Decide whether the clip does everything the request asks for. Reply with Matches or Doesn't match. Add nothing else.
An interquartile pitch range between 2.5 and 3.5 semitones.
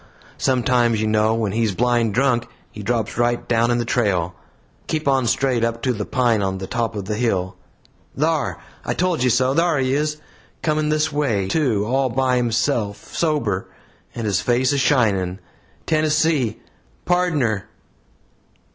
Doesn't match